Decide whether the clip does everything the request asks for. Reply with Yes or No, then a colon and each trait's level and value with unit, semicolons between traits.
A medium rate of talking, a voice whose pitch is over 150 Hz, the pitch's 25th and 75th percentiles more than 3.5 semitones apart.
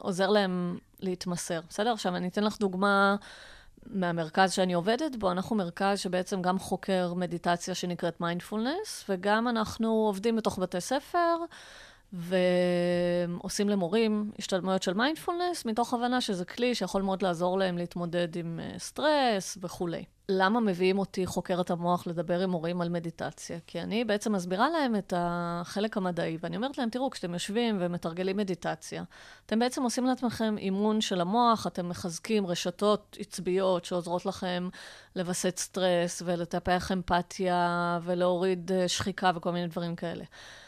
No: average, 135 wpm; medium, 185 Hz; average, 3.1 semitones